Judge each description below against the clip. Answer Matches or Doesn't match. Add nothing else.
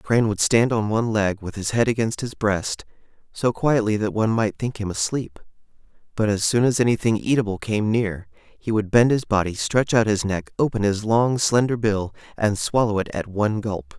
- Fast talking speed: Matches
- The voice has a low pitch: Matches